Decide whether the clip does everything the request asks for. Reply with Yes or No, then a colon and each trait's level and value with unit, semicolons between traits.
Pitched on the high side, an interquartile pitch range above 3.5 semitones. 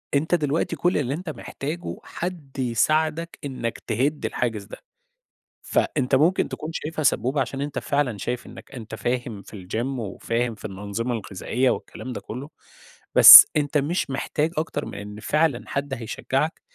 No: low, 135 Hz; average, 4.6 semitones